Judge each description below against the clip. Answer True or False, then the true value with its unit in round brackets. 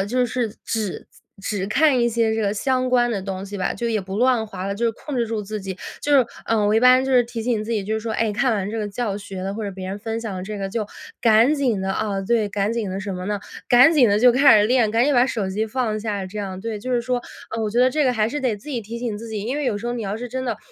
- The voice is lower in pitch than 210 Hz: False (220 Hz)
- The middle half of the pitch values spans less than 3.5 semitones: True (3.1 semitones)